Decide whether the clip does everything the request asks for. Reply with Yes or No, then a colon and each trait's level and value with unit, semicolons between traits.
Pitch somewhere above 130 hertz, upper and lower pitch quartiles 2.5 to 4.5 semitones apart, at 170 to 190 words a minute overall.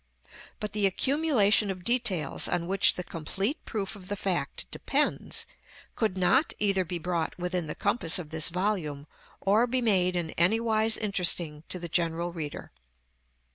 No: medium, 185 Hz; average, 3.7 semitones; average, 155 wpm